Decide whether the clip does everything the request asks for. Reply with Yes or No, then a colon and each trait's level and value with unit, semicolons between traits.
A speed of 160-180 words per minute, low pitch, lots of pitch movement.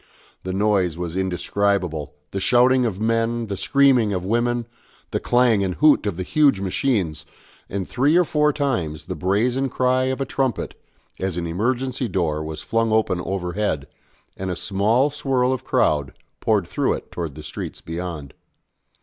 Yes: average, 165 wpm; low, 105 Hz; wide, 6.0 semitones